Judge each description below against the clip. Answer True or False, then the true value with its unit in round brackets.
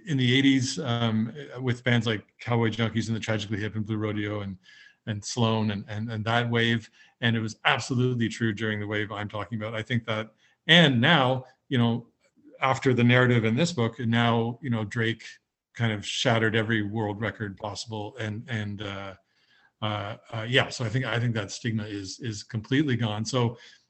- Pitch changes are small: True (2.3 semitones)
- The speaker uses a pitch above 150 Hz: False (115 Hz)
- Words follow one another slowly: False (195 wpm)